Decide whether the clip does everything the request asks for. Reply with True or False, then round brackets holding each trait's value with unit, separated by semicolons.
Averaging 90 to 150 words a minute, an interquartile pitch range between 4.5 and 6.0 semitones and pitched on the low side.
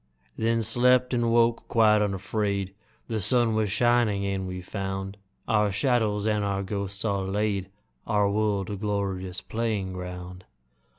False (140 wpm; 2.4 semitones; 105 Hz)